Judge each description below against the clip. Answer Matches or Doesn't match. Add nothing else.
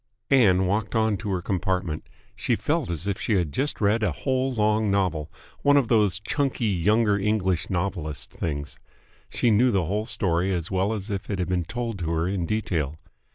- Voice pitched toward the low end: Matches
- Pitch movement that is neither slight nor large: Matches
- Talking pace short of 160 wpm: Doesn't match